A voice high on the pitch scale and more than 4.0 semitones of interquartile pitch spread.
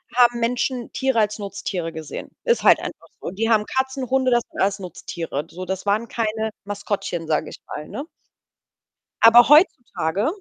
Yes: high, 220 Hz; average, 4.4 semitones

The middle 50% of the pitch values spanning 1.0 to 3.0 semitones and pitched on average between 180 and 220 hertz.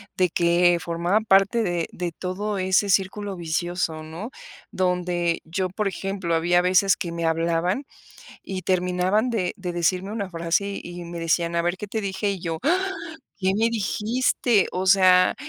Yes: narrow, 2.5 semitones; medium, 185 Hz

